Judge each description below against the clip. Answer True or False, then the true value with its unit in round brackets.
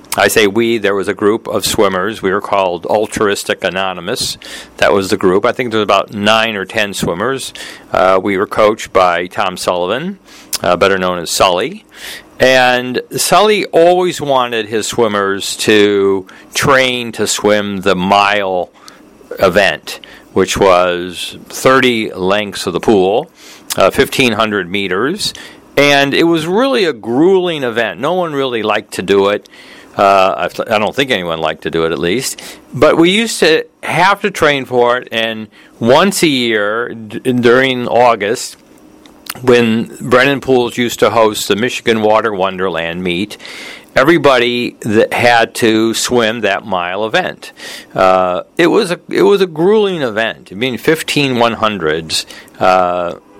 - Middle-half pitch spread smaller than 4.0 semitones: False (5.0 semitones)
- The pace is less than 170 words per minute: True (155 wpm)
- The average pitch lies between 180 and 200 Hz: False (115 Hz)